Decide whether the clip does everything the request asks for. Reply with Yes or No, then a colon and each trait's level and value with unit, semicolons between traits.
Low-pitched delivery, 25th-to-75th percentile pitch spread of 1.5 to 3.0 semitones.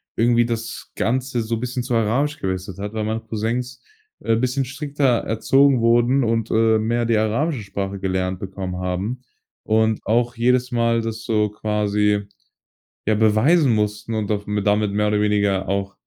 Yes: low, 110 Hz; narrow, 2.6 semitones